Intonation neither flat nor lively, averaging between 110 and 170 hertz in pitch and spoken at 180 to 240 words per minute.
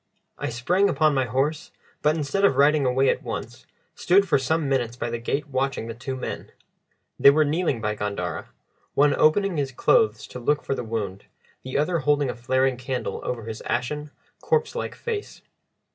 Yes: average, 4.0 semitones; low, 135 Hz; average, 185 wpm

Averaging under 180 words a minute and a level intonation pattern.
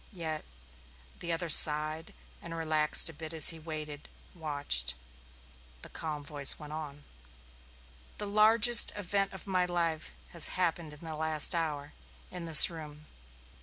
Yes: average, 140 wpm; narrow, 2.2 semitones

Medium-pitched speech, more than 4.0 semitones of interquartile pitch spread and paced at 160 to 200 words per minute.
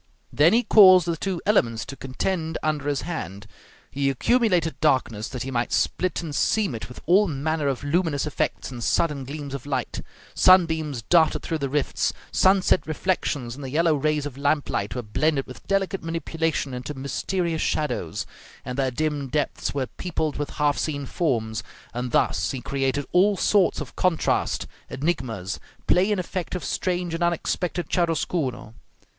Yes: medium, 150 Hz; average, 4.5 semitones; average, 165 wpm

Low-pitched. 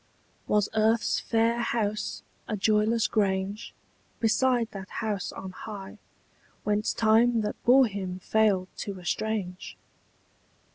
No: high, 215 Hz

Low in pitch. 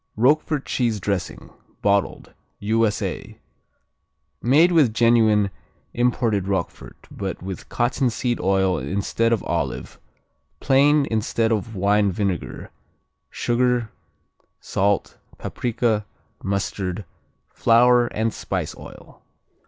Yes: low, 110 Hz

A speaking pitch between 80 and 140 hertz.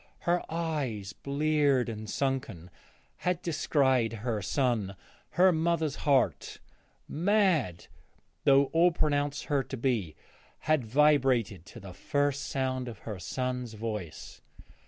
Yes: low, 135 Hz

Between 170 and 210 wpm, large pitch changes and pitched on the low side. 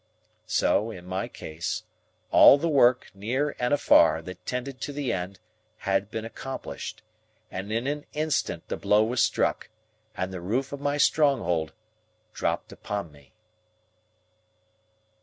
No: average, 140 wpm; wide, 6.8 semitones; low, 110 Hz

